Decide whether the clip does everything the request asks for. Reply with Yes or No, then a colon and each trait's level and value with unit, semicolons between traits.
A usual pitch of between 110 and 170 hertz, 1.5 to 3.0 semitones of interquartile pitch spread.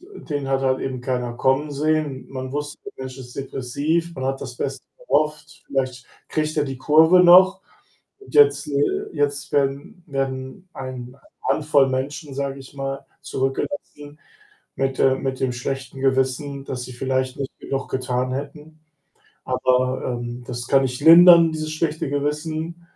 Yes: low, 135 Hz; average, 2.7 semitones